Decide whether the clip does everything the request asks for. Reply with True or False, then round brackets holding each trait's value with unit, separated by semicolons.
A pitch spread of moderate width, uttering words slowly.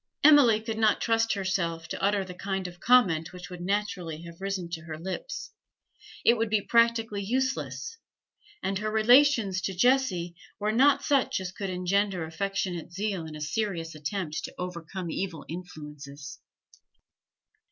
False (4.3 semitones; 150 wpm)